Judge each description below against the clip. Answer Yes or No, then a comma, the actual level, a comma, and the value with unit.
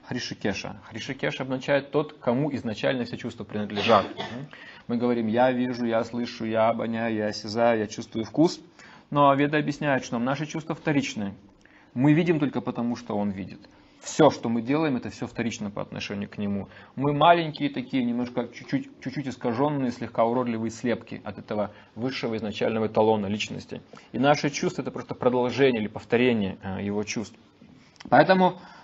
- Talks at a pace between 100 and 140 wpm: No, average, 155 wpm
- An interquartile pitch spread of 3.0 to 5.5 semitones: Yes, average, 4.1 semitones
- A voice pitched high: No, low, 120 Hz